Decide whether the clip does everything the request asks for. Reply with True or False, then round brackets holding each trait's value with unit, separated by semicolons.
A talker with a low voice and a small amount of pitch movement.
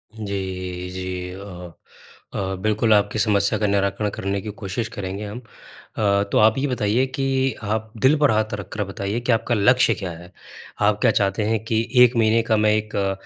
True (105 Hz; 2.1 semitones)